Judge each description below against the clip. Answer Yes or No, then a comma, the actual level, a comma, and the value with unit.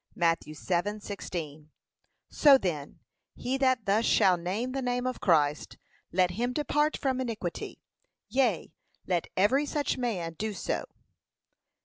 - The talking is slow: Yes, slow, 125 wpm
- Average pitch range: No, wide, 6.6 semitones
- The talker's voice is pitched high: Yes, high, 205 Hz